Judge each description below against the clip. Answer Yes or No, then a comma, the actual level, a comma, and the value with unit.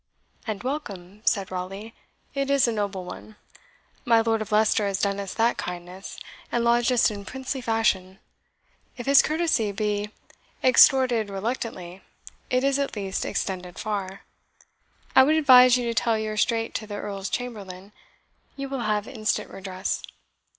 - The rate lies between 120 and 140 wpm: No, average, 155 wpm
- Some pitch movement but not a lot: Yes, average, 3.9 semitones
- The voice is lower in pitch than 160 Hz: No, high, 215 Hz